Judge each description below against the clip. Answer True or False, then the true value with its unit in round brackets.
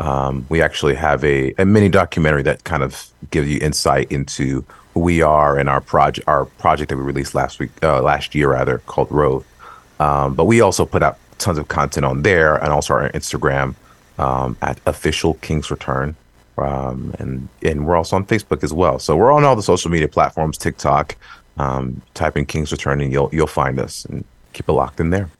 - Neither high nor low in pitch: False (75 Hz)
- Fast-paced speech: True (210 wpm)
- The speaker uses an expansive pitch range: False (2.7 semitones)